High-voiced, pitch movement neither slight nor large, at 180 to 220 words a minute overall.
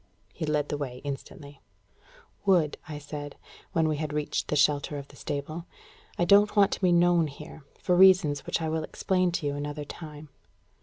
No: medium, 150 Hz; average, 3.1 semitones; average, 190 wpm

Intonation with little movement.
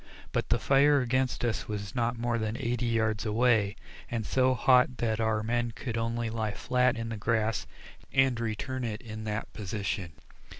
Yes: narrow, 2.1 semitones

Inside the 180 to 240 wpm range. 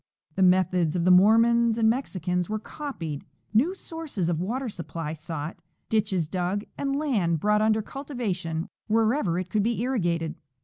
No: average, 160 wpm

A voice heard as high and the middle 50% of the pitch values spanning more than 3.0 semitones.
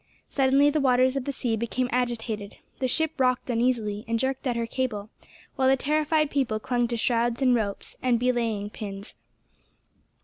No: high, 245 Hz; narrow, 2.5 semitones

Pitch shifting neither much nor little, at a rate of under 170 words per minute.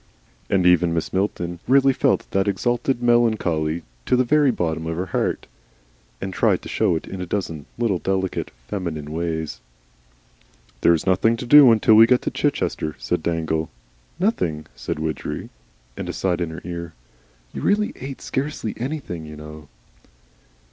No: wide, 6.7 semitones; average, 160 wpm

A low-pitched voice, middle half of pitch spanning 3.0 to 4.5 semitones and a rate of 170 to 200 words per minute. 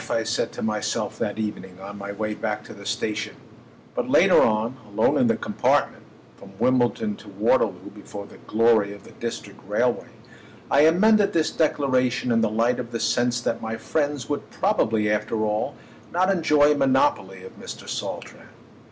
Yes: low, 115 Hz; average, 3.7 semitones; average, 175 wpm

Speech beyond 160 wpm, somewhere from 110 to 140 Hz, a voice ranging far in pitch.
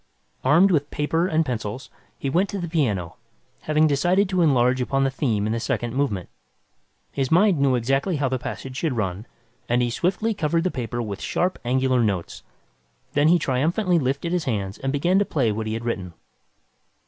Yes: average, 190 wpm; low, 135 Hz; wide, 5.7 semitones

